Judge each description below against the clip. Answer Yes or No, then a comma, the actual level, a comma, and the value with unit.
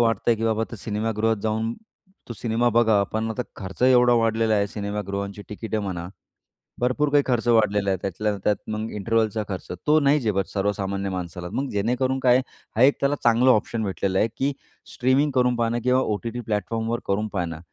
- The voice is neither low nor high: No, low, 110 Hz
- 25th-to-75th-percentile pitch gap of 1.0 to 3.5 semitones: Yes, average, 2.9 semitones